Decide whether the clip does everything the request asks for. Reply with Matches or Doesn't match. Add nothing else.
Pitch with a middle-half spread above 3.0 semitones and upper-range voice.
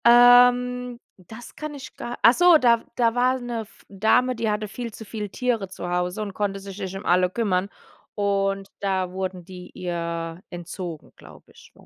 Matches